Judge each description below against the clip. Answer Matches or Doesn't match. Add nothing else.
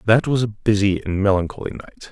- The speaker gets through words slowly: Doesn't match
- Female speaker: Doesn't match